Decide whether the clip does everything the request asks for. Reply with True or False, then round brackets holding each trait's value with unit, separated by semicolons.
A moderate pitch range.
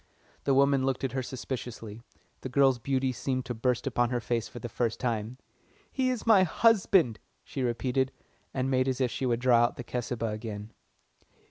False (2.2 semitones)